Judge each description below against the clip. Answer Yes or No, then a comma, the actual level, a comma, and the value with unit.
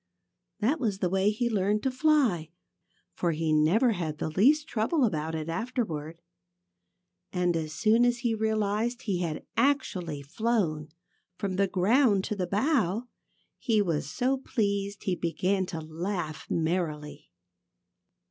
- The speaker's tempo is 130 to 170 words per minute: Yes, average, 150 wpm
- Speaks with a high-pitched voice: Yes, high, 195 Hz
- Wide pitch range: Yes, wide, 5.7 semitones